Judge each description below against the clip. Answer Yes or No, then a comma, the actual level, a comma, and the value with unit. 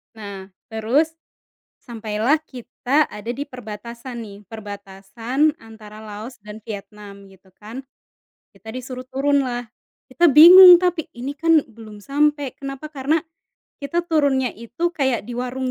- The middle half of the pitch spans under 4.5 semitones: No, average, 4.8 semitones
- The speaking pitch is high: Yes, very high, 250 Hz